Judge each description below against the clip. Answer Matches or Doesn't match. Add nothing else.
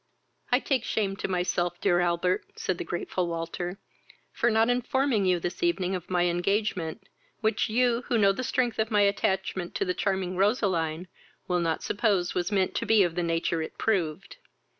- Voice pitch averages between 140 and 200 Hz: Matches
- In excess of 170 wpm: Matches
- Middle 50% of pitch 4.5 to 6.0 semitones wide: Doesn't match